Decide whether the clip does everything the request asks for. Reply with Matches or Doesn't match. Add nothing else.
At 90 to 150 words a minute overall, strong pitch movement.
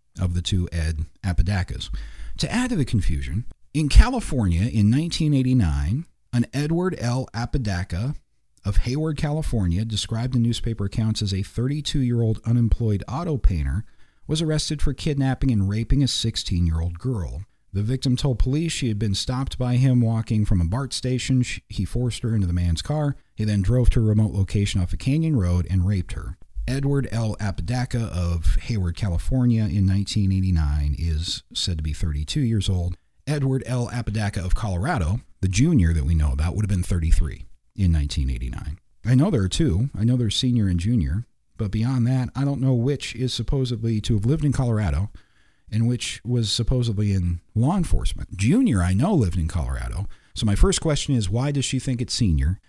Doesn't match